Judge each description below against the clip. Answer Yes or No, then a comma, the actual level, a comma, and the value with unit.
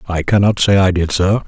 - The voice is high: No, very low, 95 Hz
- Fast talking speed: Yes, fast, 245 wpm